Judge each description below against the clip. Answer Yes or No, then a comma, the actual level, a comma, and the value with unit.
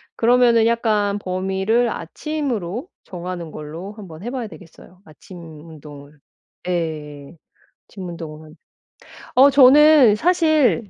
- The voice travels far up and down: Yes, wide, 6.7 semitones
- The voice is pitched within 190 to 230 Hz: Yes, high, 195 Hz